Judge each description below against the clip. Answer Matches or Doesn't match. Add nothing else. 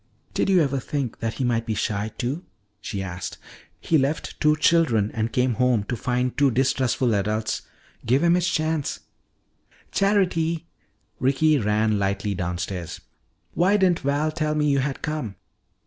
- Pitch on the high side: Doesn't match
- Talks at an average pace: Matches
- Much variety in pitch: Matches